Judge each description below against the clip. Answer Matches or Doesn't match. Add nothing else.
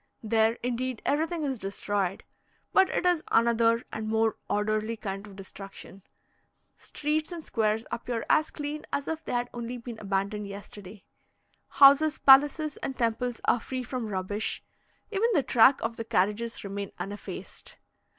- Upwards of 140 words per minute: Matches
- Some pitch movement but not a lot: Matches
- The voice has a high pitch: Matches